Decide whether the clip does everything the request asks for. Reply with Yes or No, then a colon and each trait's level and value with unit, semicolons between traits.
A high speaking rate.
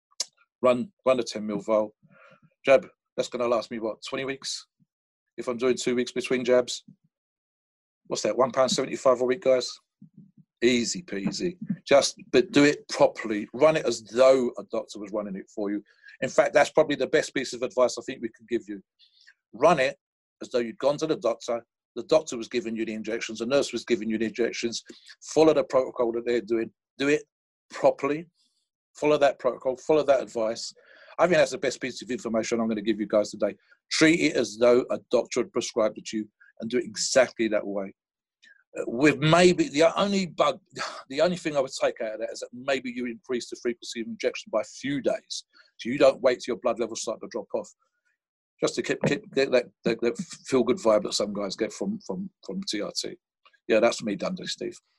Yes: fast, 215 wpm